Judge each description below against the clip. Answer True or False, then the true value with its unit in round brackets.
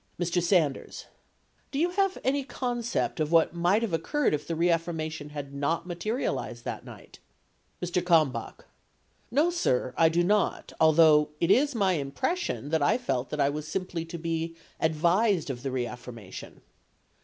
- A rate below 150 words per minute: False (165 wpm)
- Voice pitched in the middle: True (165 Hz)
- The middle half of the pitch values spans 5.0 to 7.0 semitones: True (5.4 semitones)